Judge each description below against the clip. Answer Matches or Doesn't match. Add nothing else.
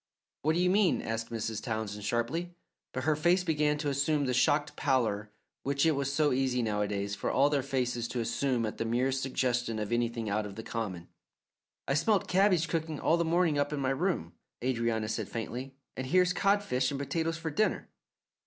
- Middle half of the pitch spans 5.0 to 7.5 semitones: Matches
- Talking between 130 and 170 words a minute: Doesn't match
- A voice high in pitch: Doesn't match